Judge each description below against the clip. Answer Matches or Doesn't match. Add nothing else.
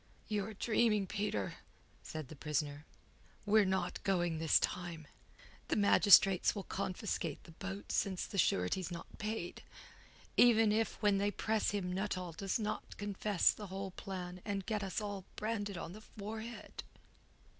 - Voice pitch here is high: Matches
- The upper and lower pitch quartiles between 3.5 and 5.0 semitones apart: Doesn't match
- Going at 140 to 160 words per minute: Matches